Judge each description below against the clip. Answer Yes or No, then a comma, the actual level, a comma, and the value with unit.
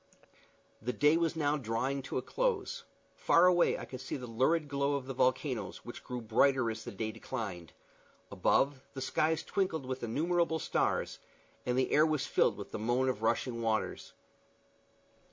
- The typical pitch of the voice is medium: No, low, 130 Hz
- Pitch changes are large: No, average, 4.8 semitones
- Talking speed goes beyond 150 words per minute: Yes, average, 170 wpm